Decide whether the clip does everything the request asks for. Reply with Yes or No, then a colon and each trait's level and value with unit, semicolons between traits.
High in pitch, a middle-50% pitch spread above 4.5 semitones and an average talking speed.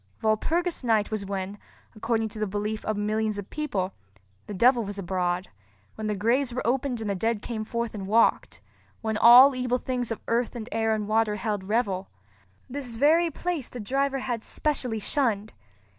No: high, 220 Hz; average, 3.2 semitones; average, 175 wpm